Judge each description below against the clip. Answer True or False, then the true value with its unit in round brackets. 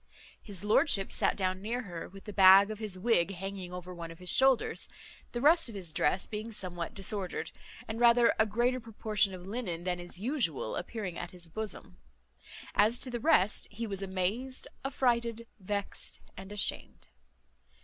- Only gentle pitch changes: False (4.1 semitones)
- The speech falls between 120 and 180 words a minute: True (170 wpm)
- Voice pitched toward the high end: True (200 Hz)